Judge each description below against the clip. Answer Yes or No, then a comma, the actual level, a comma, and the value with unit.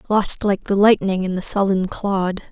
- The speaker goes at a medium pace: Yes, average, 190 wpm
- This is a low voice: No, high, 195 Hz